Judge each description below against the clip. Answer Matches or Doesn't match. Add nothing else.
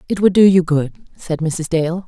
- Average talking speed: Doesn't match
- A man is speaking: Doesn't match